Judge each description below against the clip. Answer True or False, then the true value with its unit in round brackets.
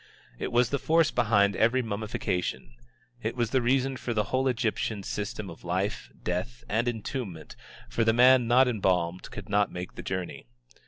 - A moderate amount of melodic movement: True (3.8 semitones)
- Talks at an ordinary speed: True (170 wpm)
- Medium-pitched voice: False (110 Hz)